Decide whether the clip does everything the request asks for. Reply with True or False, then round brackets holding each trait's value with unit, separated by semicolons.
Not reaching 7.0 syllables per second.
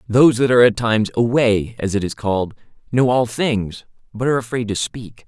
True (5.7 syllables/s)